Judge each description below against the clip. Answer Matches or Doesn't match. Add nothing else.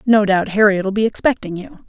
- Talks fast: Doesn't match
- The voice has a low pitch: Doesn't match